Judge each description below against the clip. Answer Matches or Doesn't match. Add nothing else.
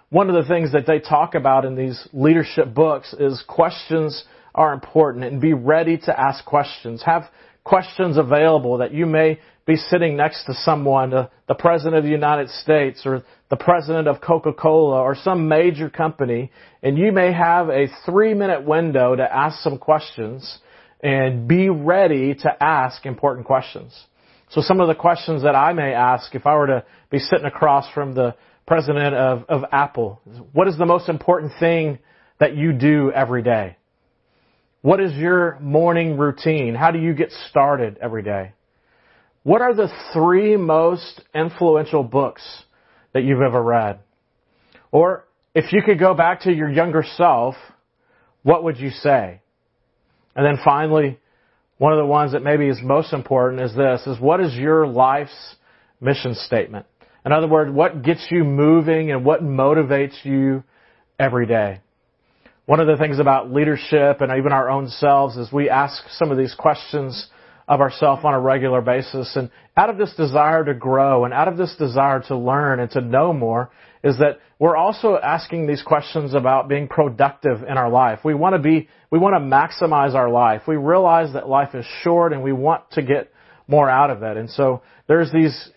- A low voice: Doesn't match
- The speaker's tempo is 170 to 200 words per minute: Matches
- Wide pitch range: Doesn't match